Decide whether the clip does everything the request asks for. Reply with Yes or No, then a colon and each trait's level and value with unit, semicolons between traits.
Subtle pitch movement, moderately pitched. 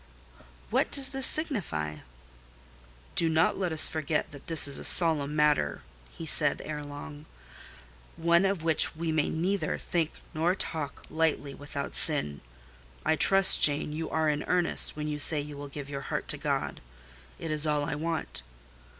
Yes: narrow, 2.2 semitones; medium, 155 Hz